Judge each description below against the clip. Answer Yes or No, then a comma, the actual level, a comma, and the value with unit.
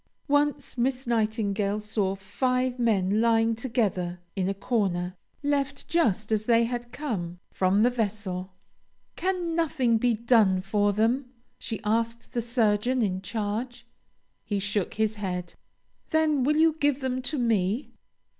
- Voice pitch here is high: Yes, high, 225 Hz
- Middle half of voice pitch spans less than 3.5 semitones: No, average, 4.0 semitones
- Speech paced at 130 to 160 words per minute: Yes, average, 140 wpm